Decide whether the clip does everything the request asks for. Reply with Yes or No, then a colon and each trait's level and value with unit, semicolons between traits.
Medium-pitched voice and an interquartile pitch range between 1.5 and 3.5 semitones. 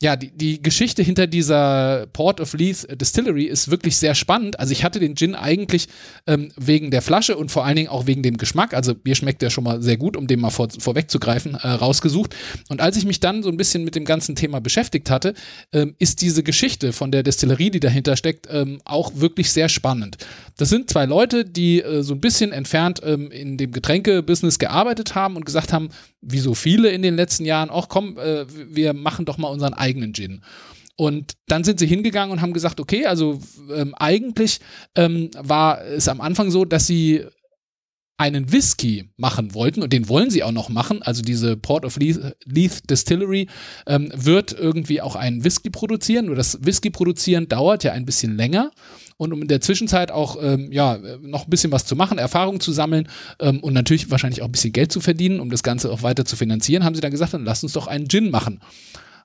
No: medium, 155 Hz; average, 4.5 semitones